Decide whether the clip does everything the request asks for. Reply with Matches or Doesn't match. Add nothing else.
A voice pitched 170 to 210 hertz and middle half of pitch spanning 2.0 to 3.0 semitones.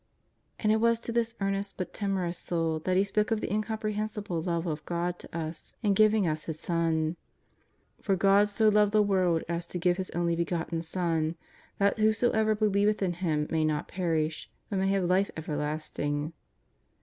Doesn't match